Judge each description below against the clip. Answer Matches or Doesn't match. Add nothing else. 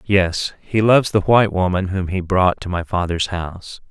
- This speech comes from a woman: Doesn't match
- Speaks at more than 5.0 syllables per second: Doesn't match